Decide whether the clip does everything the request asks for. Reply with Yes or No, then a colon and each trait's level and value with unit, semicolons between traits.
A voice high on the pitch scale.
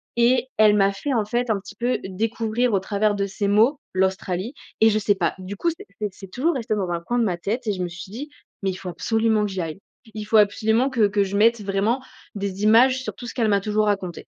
Yes: high, 210 Hz